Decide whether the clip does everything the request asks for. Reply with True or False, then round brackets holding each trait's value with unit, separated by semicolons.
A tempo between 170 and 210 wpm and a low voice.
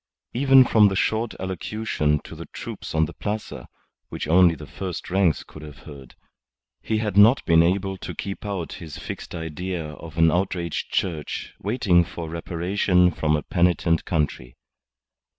False (160 wpm; 90 Hz)